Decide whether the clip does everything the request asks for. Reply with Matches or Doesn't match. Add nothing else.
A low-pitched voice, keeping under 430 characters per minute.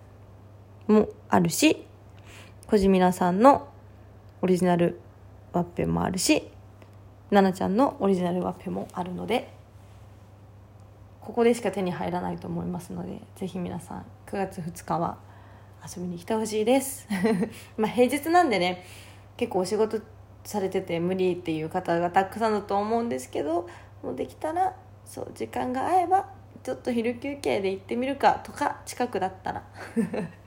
Doesn't match